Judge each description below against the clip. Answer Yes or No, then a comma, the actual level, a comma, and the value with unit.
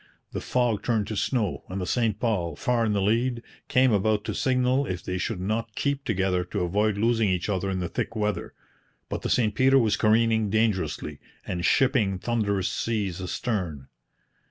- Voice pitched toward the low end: Yes, low, 110 Hz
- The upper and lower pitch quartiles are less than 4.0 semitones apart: Yes, average, 3.6 semitones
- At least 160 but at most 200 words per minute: Yes, average, 180 wpm